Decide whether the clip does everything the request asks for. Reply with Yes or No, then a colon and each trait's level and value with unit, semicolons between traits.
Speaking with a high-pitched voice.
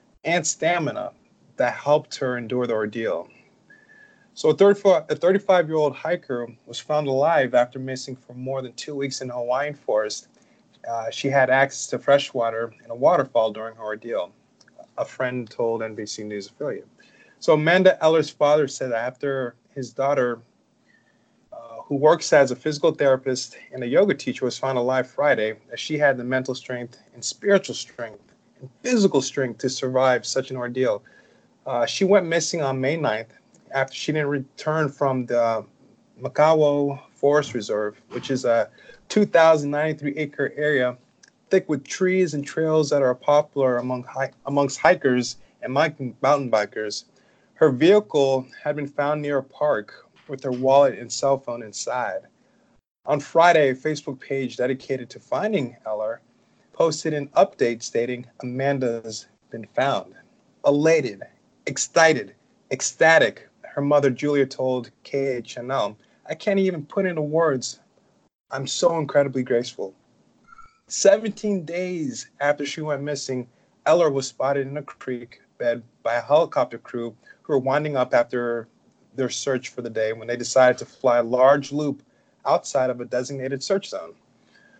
No: low, 135 Hz